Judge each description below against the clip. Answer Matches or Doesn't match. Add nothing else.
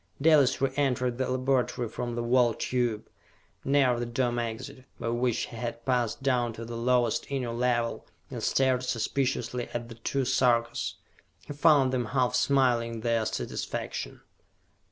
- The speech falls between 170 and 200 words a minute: Doesn't match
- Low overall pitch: Matches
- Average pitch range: Doesn't match